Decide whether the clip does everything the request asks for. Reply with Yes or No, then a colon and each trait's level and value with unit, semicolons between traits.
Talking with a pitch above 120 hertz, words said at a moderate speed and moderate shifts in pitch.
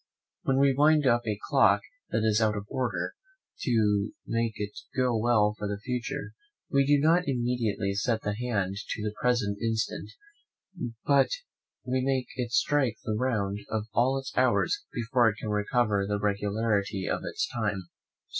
No: low, 115 Hz; average, 165 wpm; average, 3.6 semitones